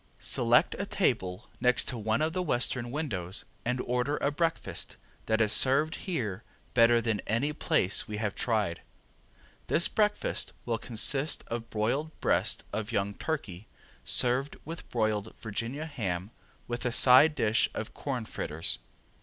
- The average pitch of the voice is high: No, low, 120 Hz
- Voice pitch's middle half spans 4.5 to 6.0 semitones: Yes, average, 5.1 semitones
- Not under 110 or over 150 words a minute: Yes, average, 145 wpm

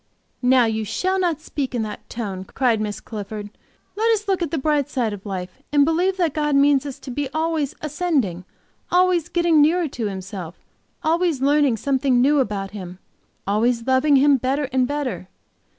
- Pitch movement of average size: No, wide, 6.1 semitones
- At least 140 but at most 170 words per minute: No, average, 180 wpm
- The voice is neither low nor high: No, very high, 270 Hz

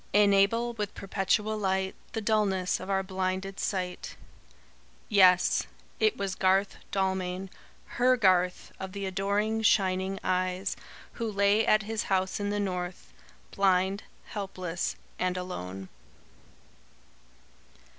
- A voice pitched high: Yes, high, 195 Hz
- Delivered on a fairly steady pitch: Yes, narrow, 1.8 semitones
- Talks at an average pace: No, slow, 115 wpm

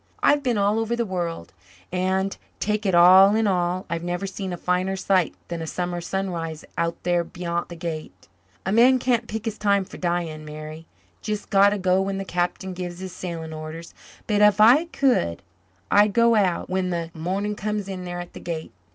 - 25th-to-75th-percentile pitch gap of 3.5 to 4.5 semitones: No, average, 3.1 semitones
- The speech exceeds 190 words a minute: Yes, average, 200 wpm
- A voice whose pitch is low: No, medium, 185 Hz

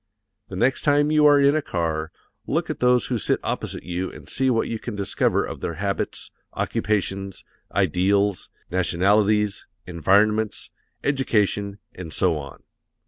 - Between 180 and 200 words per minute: No, average, 145 wpm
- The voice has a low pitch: Yes, low, 100 Hz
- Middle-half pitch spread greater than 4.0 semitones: Yes, average, 4.9 semitones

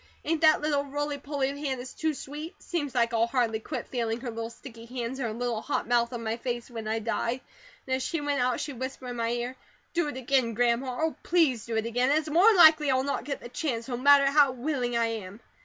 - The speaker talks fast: Yes, fast, 245 wpm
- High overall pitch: Yes, very high, 255 Hz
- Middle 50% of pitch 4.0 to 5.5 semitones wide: No, average, 3.5 semitones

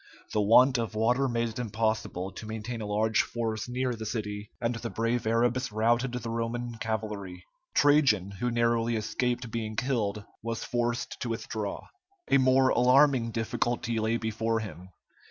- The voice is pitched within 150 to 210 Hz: No, low, 115 Hz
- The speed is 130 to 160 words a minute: Yes, average, 155 wpm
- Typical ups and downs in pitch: No, narrow, 2.0 semitones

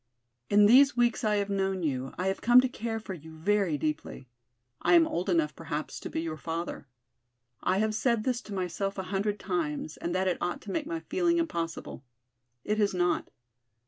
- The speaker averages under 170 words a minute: No, average, 200 wpm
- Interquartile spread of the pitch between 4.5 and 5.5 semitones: Yes, average, 4.8 semitones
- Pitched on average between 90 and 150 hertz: No, high, 195 Hz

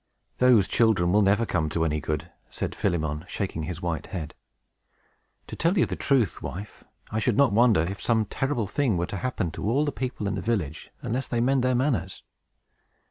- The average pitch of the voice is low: Yes, low, 105 Hz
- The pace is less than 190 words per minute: No, average, 195 wpm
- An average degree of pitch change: No, wide, 6.2 semitones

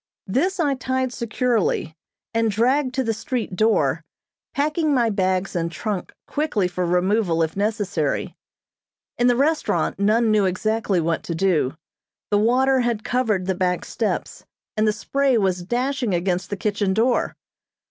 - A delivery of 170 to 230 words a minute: No, average, 150 wpm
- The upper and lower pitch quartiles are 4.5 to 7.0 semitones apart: Yes, average, 5.3 semitones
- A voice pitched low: No, high, 215 Hz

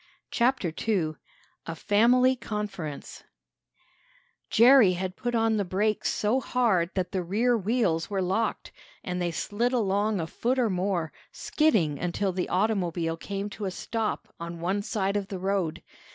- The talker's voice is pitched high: Yes, high, 200 Hz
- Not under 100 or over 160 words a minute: Yes, average, 150 wpm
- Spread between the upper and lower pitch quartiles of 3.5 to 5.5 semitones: Yes, average, 3.9 semitones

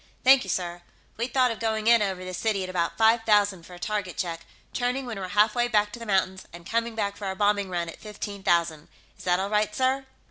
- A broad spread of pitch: No, average, 3.5 semitones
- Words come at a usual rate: No, fast, 250 wpm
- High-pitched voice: Yes, high, 205 Hz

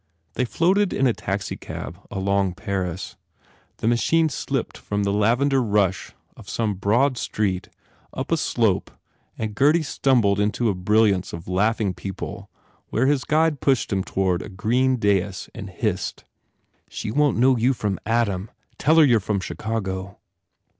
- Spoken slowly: No, average, 155 wpm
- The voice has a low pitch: Yes, low, 105 Hz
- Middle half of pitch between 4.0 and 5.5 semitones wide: Yes, average, 4.7 semitones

